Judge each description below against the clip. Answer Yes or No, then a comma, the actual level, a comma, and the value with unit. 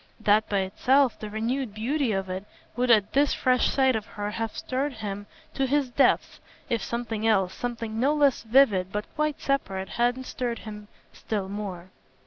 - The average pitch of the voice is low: No, high, 225 Hz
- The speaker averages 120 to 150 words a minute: No, average, 175 wpm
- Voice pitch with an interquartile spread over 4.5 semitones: No, average, 4.0 semitones